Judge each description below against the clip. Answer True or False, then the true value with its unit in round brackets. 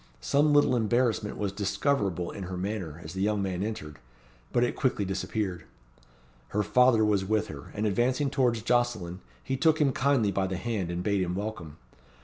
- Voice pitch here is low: True (105 Hz)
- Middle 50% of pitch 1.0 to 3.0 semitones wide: False (4.5 semitones)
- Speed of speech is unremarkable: True (180 wpm)